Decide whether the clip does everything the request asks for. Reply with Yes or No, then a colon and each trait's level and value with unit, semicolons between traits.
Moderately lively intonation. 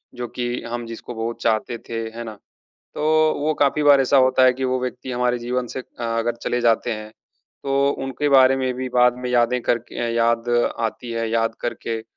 No: narrow, 1.8 semitones